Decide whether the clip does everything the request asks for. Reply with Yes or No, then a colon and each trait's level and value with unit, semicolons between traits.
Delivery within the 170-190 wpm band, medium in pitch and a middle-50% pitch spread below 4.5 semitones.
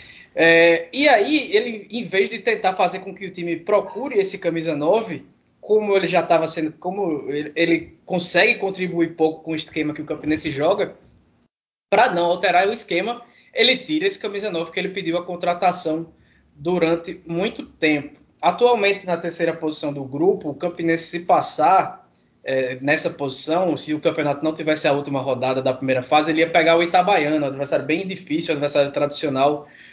Yes: average, 180 wpm; medium, 165 Hz; average, 3.5 semitones